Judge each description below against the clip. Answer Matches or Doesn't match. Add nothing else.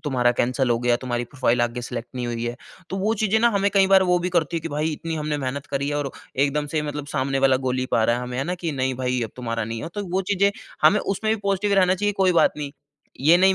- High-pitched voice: Doesn't match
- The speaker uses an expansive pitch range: Matches